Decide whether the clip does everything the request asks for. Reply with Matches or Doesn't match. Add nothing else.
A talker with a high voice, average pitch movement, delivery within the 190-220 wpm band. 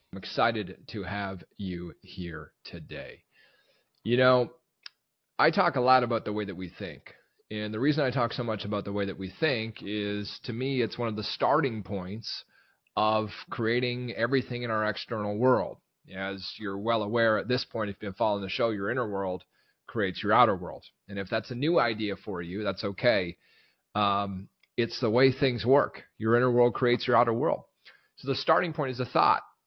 Doesn't match